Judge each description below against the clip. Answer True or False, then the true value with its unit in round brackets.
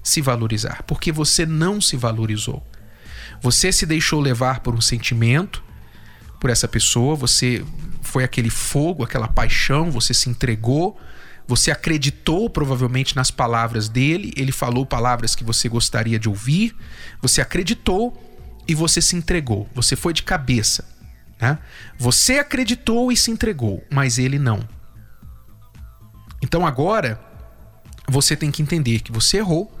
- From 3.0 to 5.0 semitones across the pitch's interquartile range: False (5.6 semitones)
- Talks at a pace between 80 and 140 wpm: True (135 wpm)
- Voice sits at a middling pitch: False (130 Hz)